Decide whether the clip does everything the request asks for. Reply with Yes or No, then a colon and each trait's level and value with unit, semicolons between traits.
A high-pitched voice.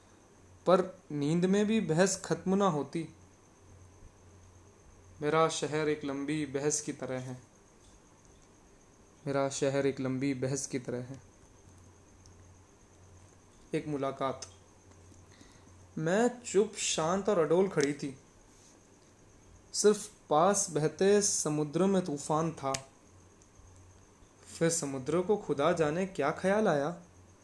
No: low, 135 Hz